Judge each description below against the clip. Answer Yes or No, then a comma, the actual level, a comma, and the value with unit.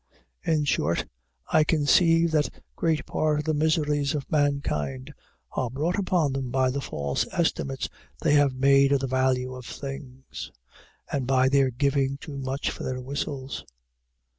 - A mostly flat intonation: Yes, narrow, 2.3 semitones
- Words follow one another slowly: No, average, 155 wpm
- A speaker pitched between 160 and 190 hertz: No, medium, 140 Hz